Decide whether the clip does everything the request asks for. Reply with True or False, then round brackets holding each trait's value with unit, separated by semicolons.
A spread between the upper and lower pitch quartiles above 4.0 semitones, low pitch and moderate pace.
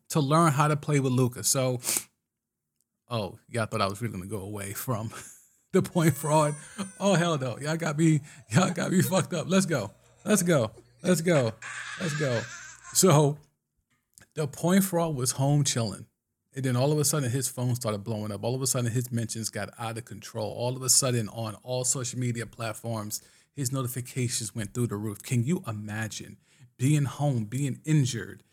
True (5.2 semitones; 130 Hz; 190 wpm)